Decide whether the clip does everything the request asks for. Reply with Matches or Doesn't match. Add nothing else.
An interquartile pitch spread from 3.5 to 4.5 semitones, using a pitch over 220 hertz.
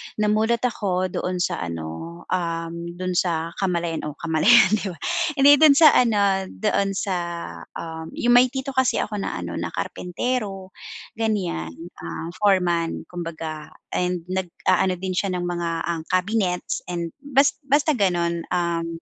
Doesn't match